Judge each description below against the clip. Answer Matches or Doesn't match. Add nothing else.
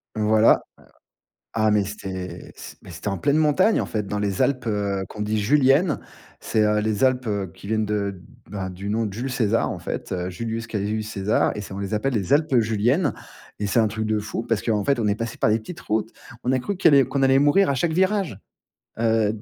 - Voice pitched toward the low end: Matches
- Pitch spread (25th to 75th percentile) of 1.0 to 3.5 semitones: Doesn't match